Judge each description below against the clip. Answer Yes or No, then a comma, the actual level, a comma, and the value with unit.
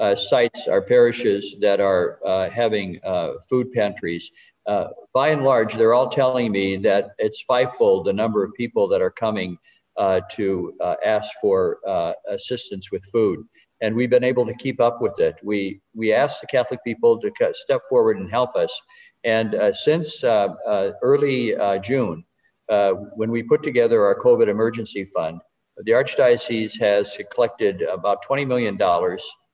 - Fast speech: No, average, 170 wpm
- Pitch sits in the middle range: No, low, 130 Hz